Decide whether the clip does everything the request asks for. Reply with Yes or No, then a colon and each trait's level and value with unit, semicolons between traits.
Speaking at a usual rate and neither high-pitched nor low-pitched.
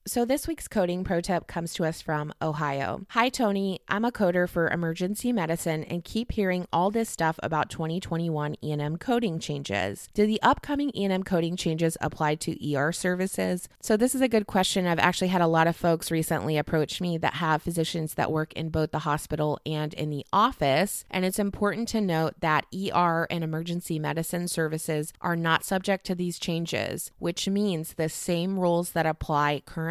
Yes: average, 190 wpm; medium, 170 Hz